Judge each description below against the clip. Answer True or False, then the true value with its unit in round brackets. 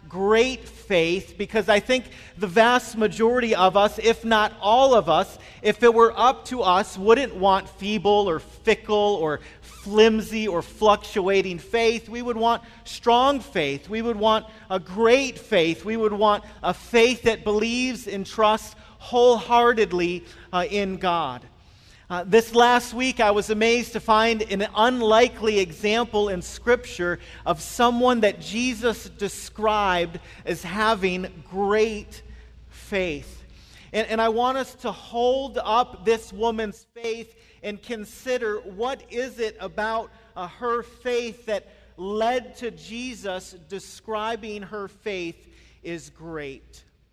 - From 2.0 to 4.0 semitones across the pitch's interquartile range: True (3.1 semitones)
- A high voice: True (215 Hz)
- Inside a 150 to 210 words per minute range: False (135 wpm)